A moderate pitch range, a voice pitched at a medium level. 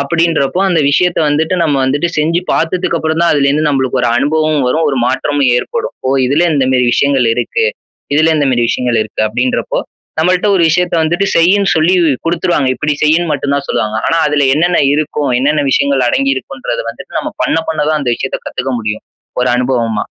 Yes: average, 4.1 semitones; medium, 150 Hz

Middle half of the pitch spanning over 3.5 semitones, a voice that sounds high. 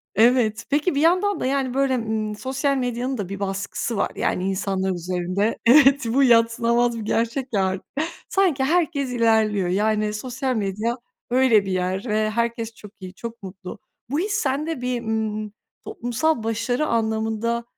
Yes: average, 3.9 semitones; high, 230 Hz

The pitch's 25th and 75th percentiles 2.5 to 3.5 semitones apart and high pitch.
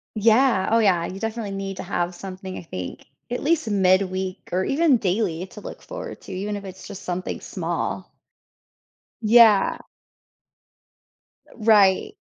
Yes: average, 3.2 semitones; high, 195 Hz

